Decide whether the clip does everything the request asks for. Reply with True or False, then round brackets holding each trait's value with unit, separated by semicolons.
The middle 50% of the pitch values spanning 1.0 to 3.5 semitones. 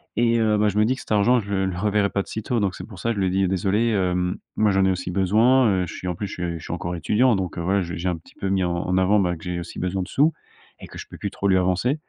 True (2.8 semitones)